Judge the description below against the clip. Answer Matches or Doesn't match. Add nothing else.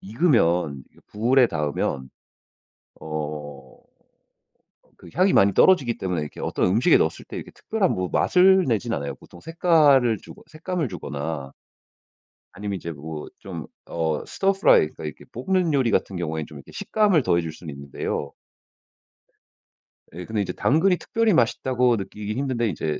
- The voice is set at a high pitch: Doesn't match